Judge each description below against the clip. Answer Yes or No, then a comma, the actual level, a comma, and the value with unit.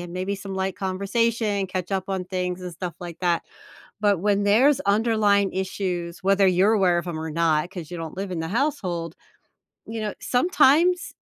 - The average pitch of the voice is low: No, high, 190 Hz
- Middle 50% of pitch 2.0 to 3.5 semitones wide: Yes, average, 2.8 semitones